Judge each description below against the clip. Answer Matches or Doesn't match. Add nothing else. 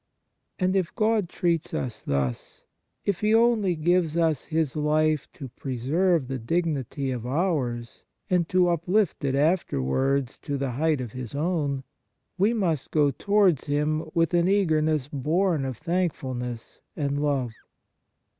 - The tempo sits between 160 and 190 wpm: Doesn't match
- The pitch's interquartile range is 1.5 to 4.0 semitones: Doesn't match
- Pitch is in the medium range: Matches